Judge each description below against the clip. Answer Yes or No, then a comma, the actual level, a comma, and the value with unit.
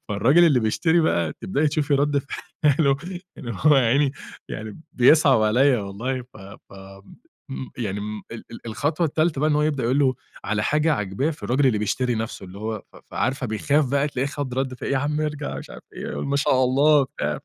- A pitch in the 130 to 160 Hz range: Yes, low, 135 Hz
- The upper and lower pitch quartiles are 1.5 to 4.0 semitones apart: No, average, 4.9 semitones